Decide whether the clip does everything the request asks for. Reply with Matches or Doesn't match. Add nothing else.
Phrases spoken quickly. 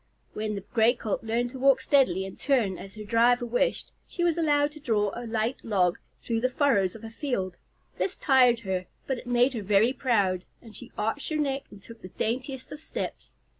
Matches